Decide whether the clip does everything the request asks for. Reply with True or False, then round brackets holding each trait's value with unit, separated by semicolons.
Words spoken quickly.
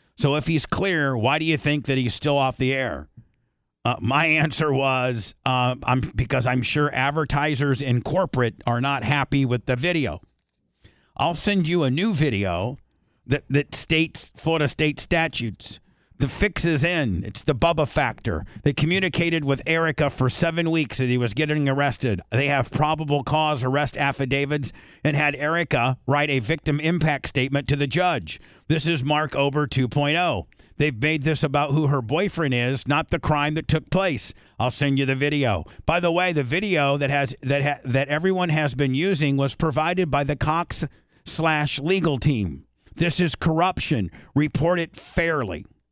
False (175 wpm)